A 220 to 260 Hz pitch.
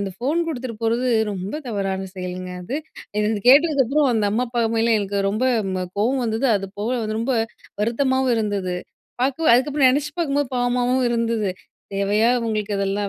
Yes: high, 230 Hz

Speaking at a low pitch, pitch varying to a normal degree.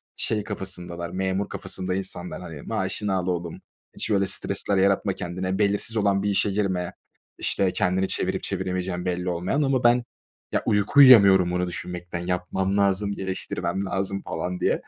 No: very low, 95 Hz; narrow, 1.8 semitones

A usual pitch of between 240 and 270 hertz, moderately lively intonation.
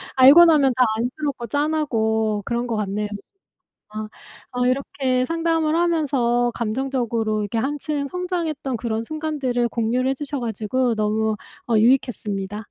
Yes: very high, 250 Hz; average, 4.6 semitones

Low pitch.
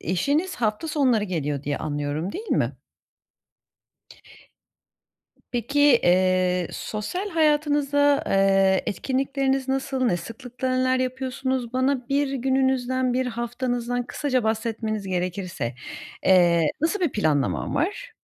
No: high, 245 Hz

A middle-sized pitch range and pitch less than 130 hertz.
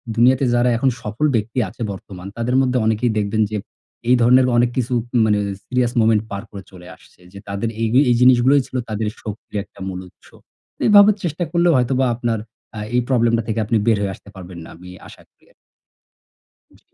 Yes: average, 3.3 semitones; low, 115 Hz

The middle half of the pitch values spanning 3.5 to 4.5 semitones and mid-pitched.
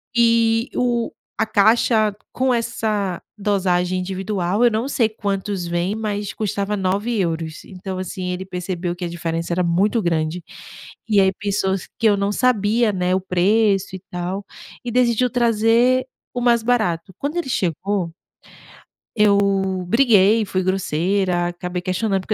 No: average, 3.8 semitones; high, 200 Hz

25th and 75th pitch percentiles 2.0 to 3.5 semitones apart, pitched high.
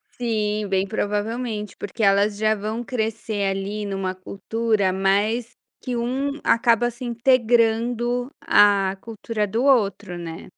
Yes: average, 2.8 semitones; high, 215 Hz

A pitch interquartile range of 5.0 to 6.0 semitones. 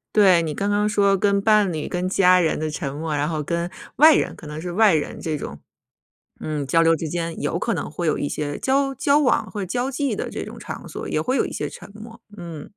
Yes: average, 5.3 semitones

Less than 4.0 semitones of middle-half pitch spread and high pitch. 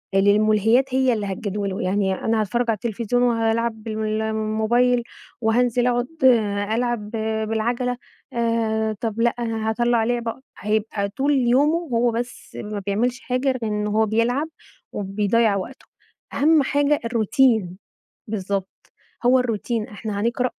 Yes: narrow, 2.4 semitones; high, 225 Hz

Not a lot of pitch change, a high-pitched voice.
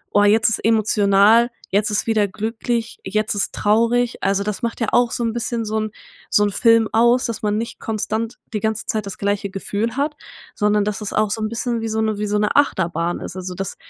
Yes: narrow, 2.0 semitones; high, 215 Hz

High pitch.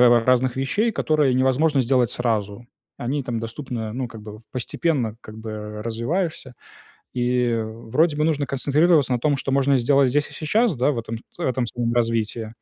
No: low, 125 Hz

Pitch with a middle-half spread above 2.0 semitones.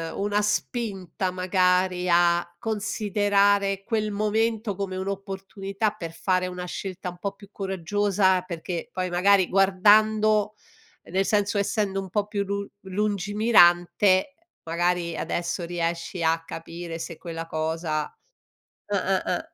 Yes: average, 2.7 semitones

